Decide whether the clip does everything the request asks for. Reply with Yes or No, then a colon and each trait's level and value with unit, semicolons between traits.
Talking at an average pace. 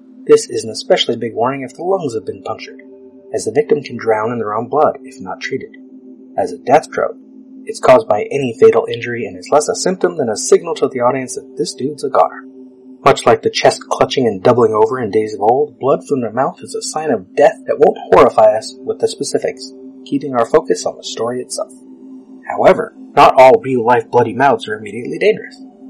No: fast, 220 wpm